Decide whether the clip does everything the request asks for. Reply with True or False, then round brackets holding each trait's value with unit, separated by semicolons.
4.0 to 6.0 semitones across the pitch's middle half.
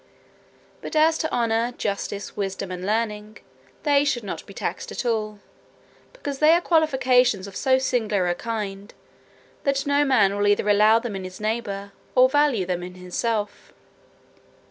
True (4.8 semitones)